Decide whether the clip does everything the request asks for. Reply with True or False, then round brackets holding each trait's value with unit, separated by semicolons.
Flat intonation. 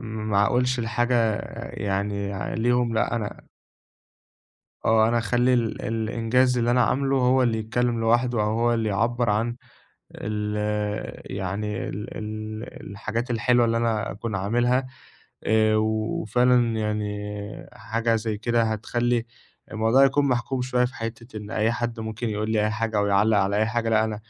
True (2.1 semitones)